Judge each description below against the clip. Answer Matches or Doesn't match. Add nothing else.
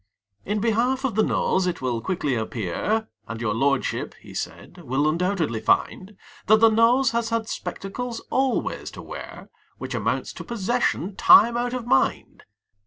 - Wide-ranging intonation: Matches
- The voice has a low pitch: Doesn't match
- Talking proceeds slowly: Doesn't match